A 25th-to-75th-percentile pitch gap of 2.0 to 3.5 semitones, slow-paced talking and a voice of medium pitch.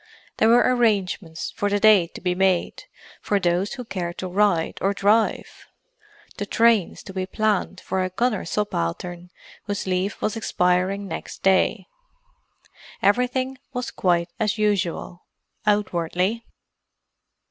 No: average, 3.2 semitones; slow, 130 wpm; high, 195 Hz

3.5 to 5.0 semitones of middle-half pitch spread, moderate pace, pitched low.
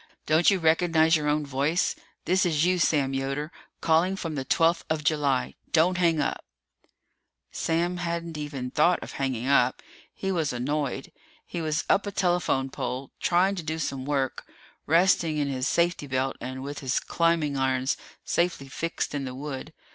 No: average, 3.8 semitones; average, 170 wpm; medium, 155 Hz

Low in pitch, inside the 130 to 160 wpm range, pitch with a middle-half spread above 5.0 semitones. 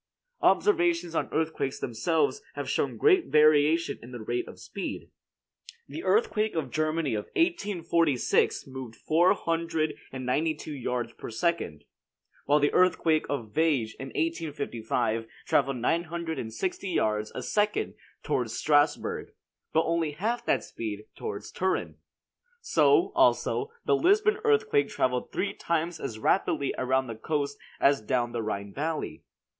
No: medium, 155 Hz; average, 140 wpm; wide, 5.5 semitones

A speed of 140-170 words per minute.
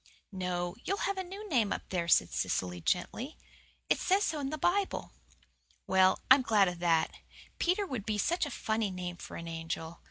No: average, 190 wpm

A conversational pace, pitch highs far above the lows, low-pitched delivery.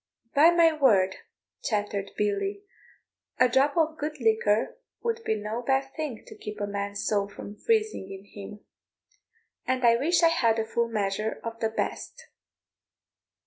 No: average, 155 wpm; wide, 6.8 semitones; high, 230 Hz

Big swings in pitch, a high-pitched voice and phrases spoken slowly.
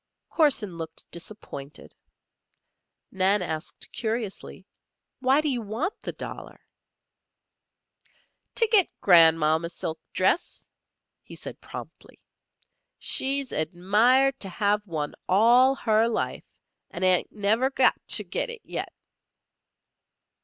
Yes: wide, 7.0 semitones; high, 210 Hz; slow, 110 wpm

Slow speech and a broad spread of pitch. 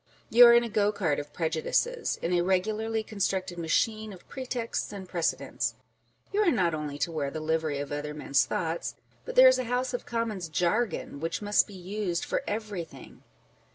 No: average, 190 wpm; wide, 5.7 semitones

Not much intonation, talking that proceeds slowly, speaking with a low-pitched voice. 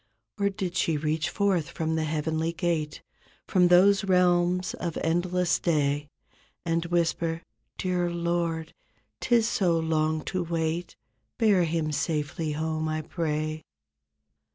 No: narrow, 2.1 semitones; slow, 125 wpm; medium, 165 Hz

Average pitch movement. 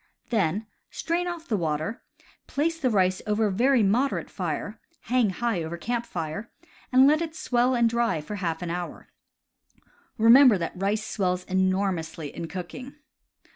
No: wide, 5.7 semitones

